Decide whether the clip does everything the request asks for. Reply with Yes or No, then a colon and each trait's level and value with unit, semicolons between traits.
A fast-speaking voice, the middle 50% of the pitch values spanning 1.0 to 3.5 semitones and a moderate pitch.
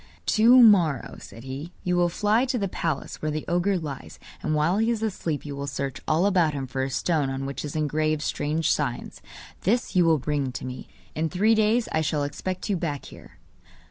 No: fast, 210 wpm; average, 4.9 semitones; medium, 155 Hz